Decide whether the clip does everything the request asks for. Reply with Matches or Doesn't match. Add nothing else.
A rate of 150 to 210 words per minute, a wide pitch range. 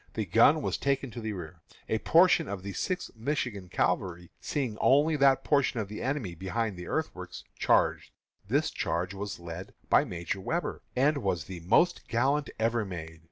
Matches